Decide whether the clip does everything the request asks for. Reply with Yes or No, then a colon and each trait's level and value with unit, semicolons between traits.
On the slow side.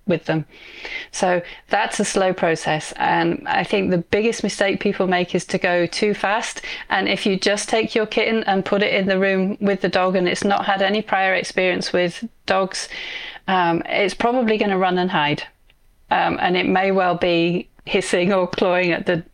No: average, 200 wpm